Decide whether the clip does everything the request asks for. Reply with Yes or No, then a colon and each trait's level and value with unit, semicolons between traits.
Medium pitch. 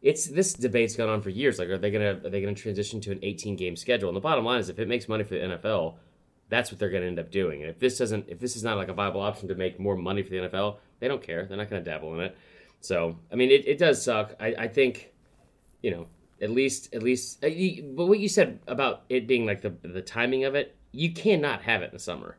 No: low, 110 Hz